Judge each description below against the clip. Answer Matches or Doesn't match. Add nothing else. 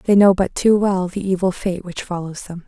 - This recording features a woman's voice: Matches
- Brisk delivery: Matches